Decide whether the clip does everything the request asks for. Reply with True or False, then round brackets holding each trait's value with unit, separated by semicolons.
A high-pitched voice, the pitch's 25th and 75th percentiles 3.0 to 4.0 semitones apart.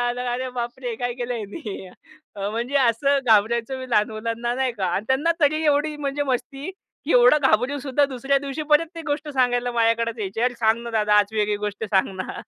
True (245 Hz; 3.6 semitones)